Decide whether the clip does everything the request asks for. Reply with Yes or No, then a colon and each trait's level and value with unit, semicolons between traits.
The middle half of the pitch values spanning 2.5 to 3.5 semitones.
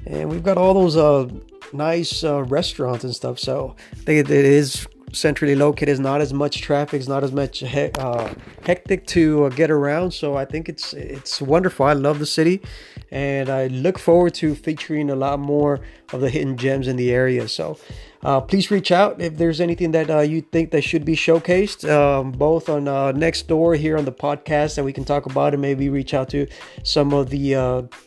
Yes: average, 2.9 semitones